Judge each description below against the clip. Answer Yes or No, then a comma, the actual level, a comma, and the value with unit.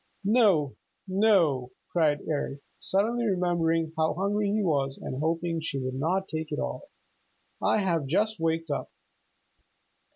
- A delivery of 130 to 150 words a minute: Yes, slow, 135 wpm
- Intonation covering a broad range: No, average, 4.6 semitones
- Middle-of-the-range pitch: Yes, medium, 165 Hz